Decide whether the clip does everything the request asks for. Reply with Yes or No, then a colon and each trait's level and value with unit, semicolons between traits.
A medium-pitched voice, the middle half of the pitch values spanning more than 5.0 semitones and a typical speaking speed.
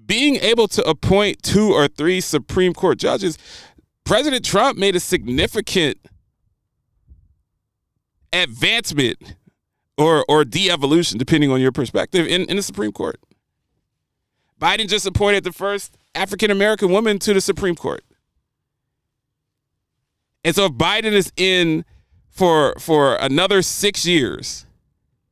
No: medium, 180 Hz; wide, 5.4 semitones; slow, 125 wpm